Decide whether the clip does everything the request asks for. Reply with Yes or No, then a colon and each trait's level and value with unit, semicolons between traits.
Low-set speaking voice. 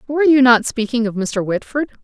No: high, 245 Hz